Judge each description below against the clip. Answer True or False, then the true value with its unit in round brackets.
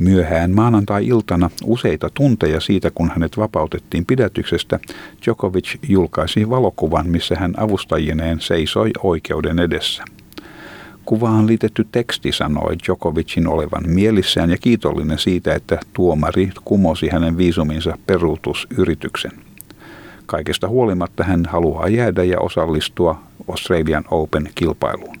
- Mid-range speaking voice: False (90 Hz)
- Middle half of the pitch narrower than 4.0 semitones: False (4.6 semitones)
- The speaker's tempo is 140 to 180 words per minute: False (100 wpm)